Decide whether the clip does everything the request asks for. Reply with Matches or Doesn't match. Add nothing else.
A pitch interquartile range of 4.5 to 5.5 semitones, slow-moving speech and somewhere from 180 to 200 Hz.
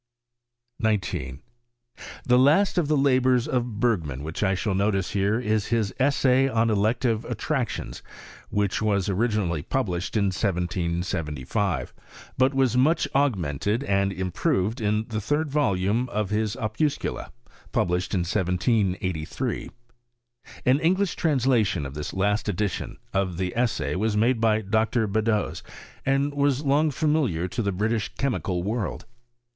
Doesn't match